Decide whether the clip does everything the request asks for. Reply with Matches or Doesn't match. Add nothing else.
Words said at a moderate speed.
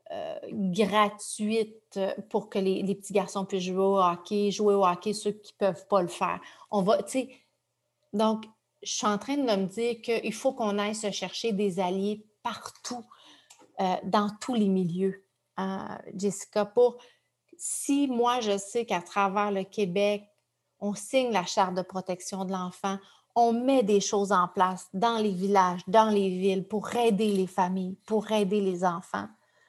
Matches